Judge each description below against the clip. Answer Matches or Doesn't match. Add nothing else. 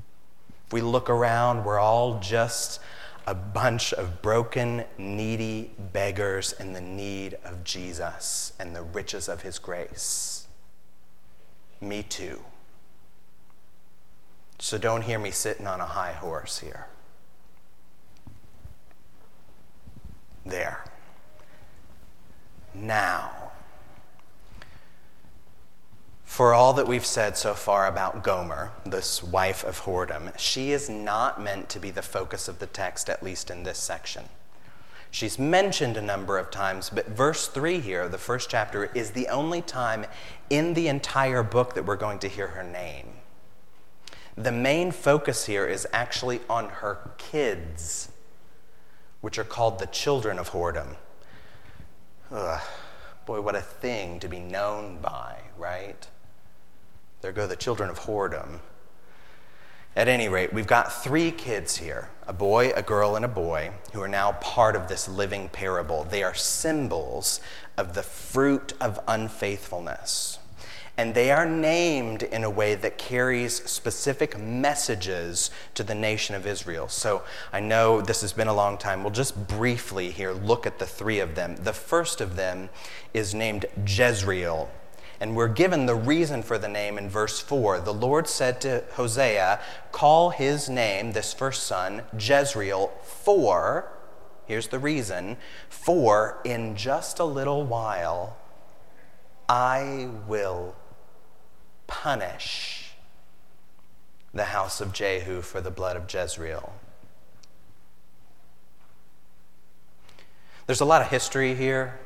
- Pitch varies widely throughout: Doesn't match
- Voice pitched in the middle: Doesn't match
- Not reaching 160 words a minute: Matches